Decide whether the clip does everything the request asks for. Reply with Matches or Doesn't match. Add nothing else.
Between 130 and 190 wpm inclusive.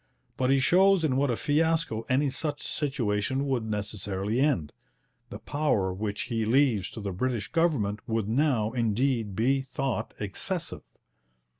Matches